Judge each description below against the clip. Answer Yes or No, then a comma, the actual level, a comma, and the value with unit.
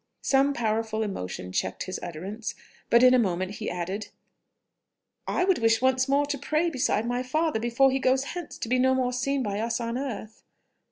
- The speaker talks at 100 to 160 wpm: No, average, 190 wpm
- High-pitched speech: Yes, high, 245 Hz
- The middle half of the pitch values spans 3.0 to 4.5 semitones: Yes, average, 3.8 semitones